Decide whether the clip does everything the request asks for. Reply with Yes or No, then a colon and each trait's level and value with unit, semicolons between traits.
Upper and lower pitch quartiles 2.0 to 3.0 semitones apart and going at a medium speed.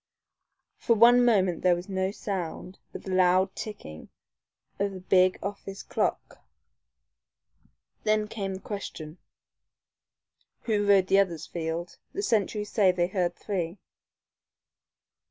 No: narrow, 2.4 semitones; slow, 120 wpm